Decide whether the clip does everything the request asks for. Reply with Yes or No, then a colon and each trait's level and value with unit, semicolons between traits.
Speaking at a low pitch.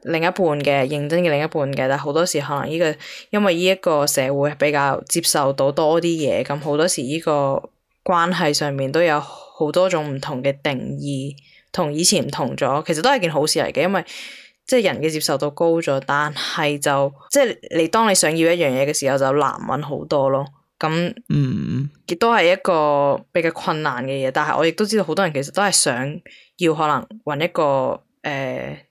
No: medium, 150 Hz